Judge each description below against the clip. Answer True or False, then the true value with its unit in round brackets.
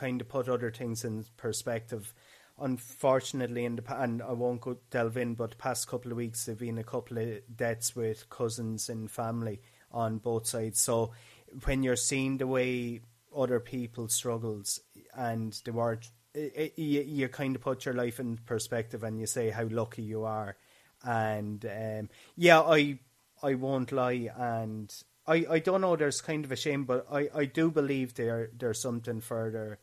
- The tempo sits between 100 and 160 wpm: False (180 wpm)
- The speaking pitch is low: True (120 Hz)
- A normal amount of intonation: False (2.3 semitones)